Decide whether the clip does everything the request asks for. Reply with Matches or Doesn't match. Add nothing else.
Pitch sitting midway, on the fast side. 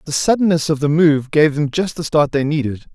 Matches